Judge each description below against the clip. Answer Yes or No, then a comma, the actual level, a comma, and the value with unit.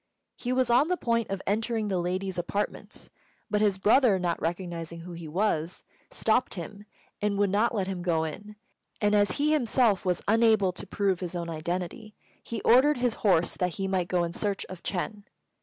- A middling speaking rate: Yes, average, 190 wpm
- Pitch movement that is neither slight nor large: Yes, average, 3.7 semitones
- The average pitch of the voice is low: No, high, 195 Hz